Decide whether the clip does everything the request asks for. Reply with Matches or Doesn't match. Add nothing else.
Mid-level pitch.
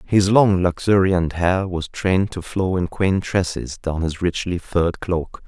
Doesn't match